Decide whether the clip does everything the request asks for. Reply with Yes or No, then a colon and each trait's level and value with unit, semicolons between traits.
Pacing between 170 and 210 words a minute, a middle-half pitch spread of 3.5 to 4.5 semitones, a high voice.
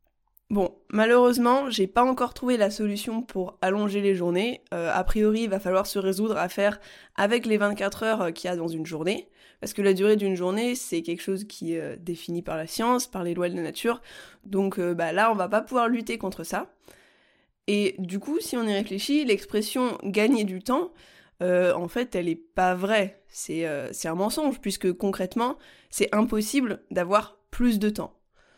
Yes: average, 200 wpm; average, 3.9 semitones; high, 200 Hz